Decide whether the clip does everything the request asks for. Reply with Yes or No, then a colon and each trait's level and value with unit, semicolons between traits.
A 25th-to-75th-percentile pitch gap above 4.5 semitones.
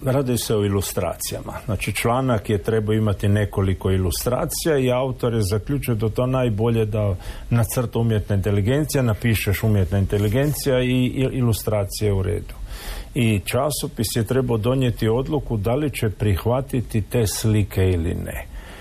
No: average, 3.4 semitones